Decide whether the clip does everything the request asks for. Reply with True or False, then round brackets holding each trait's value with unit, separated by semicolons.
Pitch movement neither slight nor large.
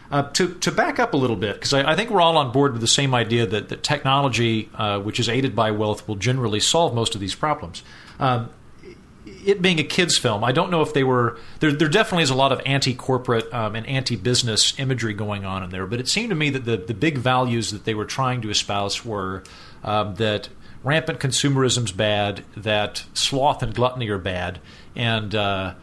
True (4.6 semitones)